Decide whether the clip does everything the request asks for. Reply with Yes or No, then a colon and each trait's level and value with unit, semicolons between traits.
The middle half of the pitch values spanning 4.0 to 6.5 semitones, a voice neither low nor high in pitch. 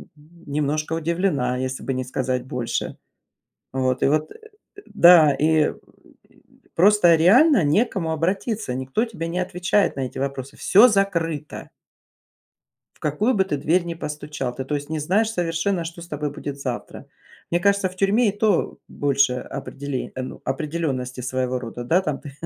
Yes: average, 5.1 semitones; medium, 155 Hz